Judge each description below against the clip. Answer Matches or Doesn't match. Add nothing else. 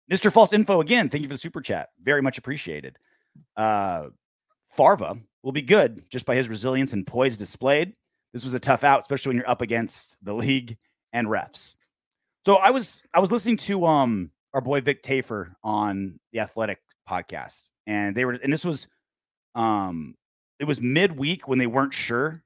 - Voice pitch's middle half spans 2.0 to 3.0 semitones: Doesn't match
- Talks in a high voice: Doesn't match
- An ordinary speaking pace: Matches